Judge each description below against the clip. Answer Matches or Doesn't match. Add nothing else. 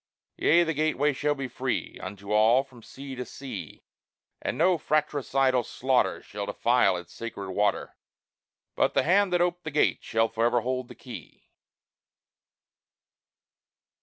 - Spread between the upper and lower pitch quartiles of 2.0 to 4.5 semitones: Doesn't match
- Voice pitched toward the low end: Matches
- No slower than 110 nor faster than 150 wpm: Matches